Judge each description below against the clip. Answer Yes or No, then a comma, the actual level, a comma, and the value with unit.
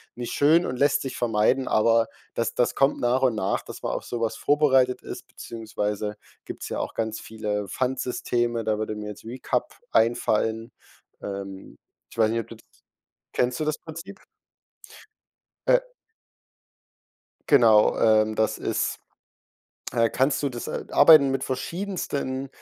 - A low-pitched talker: Yes, low, 120 Hz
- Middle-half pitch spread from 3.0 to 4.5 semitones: Yes, average, 3.5 semitones